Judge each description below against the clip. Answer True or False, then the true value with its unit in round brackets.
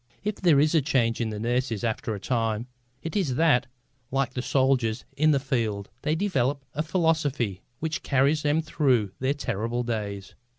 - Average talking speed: True (175 wpm)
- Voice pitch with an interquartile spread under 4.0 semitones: False (4.9 semitones)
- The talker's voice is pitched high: False (130 Hz)